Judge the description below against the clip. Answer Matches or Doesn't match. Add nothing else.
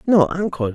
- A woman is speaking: Doesn't match